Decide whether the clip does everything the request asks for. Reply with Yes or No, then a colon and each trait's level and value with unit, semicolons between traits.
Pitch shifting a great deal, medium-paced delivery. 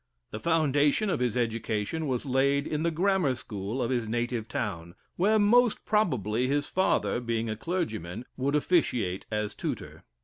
Yes: wide, 6.3 semitones; average, 160 wpm